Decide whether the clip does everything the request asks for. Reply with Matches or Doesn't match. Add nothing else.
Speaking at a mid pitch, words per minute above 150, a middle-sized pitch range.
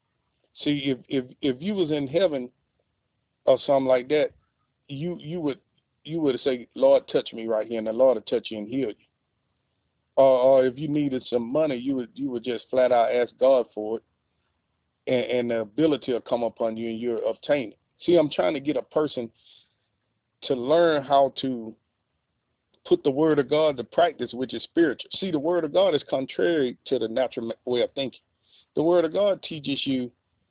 Doesn't match